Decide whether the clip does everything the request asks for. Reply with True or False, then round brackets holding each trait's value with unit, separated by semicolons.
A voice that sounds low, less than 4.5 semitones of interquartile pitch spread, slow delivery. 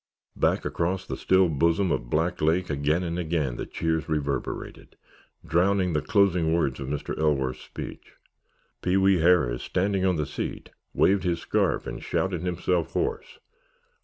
False (85 Hz; 3.3 semitones; 155 wpm)